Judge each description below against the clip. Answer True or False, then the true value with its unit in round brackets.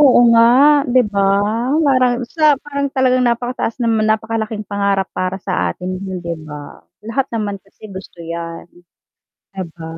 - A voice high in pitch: True (215 Hz)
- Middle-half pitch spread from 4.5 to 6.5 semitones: True (4.8 semitones)